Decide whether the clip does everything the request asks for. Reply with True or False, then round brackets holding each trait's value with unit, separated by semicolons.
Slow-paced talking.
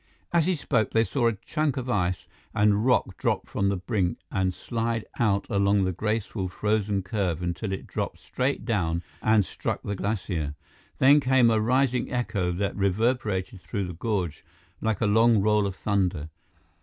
False (170 wpm)